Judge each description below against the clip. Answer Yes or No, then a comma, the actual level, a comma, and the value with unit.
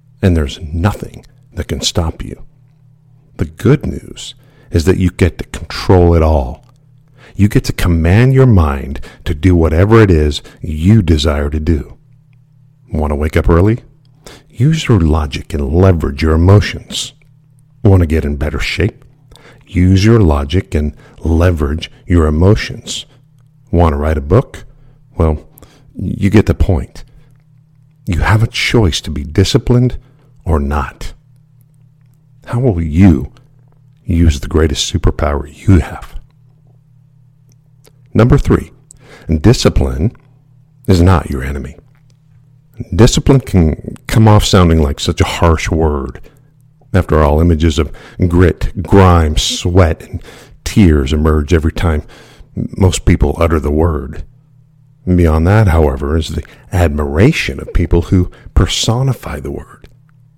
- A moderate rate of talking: No, slow, 130 wpm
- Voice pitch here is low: Yes, very low, 95 Hz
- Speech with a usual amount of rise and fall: No, wide, 8.6 semitones